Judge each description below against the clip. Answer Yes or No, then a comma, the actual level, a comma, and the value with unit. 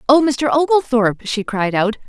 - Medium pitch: No, high, 245 Hz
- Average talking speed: Yes, average, 175 wpm